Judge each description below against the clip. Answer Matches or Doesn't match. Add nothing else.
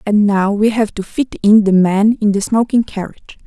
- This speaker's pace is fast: Matches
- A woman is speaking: Matches